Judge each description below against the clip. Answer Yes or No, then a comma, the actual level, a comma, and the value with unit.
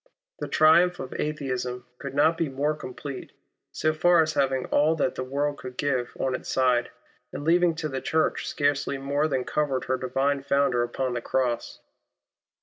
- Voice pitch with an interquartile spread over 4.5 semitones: No, average, 3.0 semitones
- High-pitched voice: No, medium, 140 Hz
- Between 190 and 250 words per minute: No, average, 175 wpm